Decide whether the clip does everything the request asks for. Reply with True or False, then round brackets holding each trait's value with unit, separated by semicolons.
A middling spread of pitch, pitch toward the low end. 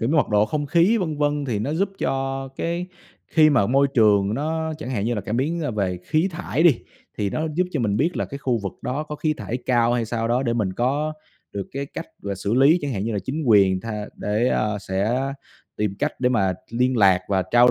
False (6.0 semitones; 125 Hz)